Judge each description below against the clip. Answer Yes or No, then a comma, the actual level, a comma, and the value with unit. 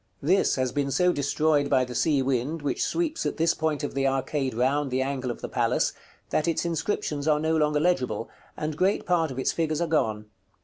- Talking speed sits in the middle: No, fast, 215 wpm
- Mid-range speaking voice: Yes, medium, 145 Hz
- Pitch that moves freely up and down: No, average, 3.2 semitones